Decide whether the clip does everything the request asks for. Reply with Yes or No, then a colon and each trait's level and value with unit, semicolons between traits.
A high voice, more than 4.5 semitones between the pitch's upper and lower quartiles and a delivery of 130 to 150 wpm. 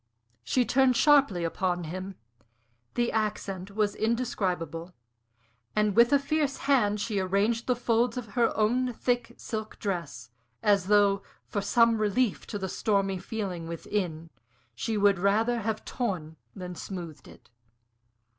No: high, 205 Hz; average, 4.1 semitones; slow, 135 wpm